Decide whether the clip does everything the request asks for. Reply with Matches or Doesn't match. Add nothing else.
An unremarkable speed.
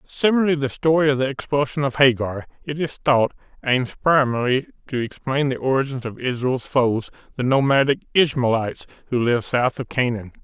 Matches